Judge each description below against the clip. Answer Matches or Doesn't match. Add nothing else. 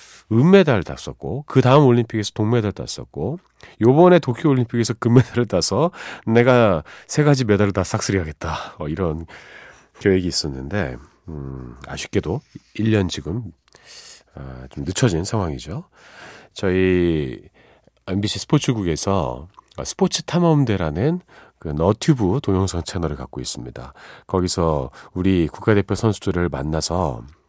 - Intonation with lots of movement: Matches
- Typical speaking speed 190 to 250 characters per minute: Doesn't match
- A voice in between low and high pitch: Doesn't match